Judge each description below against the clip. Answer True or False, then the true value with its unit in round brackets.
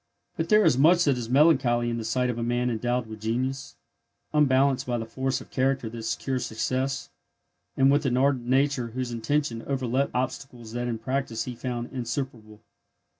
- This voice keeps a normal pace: True (180 wpm)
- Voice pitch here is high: False (125 Hz)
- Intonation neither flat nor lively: False (2.3 semitones)